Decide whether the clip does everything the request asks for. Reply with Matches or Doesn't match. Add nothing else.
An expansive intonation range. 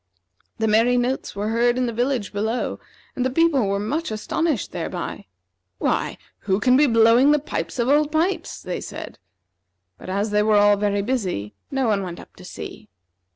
Doesn't match